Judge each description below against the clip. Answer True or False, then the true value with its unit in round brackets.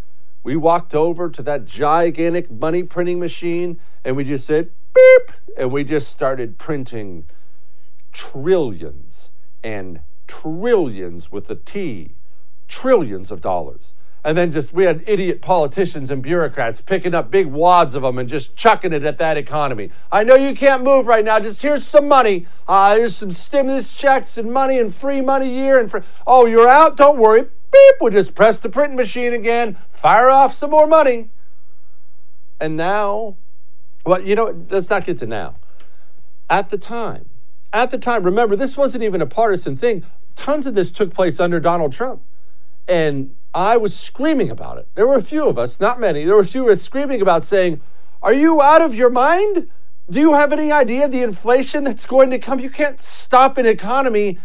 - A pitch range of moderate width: False (8.6 semitones)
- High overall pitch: True (200 Hz)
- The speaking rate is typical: True (185 wpm)